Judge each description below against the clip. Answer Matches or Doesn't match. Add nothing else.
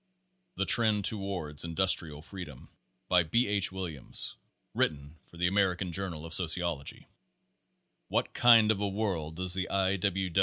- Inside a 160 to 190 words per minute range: Doesn't match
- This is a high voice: Doesn't match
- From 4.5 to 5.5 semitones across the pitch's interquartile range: Doesn't match